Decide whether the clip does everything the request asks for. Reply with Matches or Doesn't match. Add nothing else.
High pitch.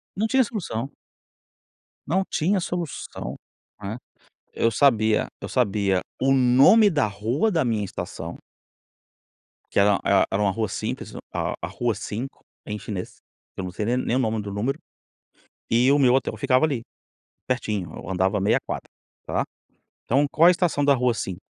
Doesn't match